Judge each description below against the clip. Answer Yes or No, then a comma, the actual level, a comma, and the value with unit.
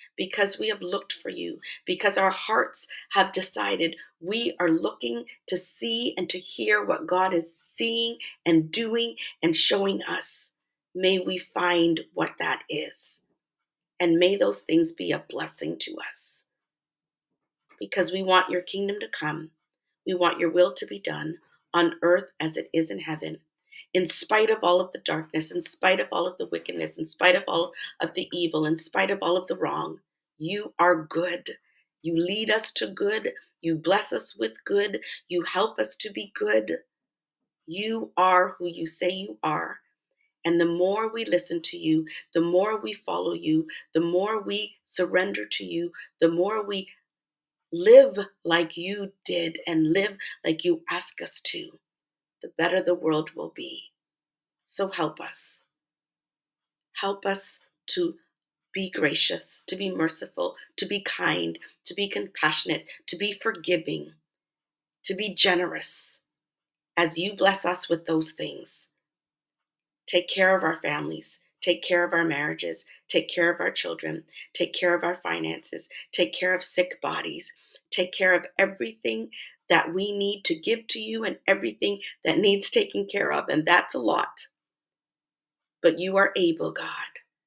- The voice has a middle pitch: Yes, medium, 180 Hz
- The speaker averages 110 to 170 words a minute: Yes, average, 165 wpm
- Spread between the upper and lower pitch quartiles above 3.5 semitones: No, average, 3.2 semitones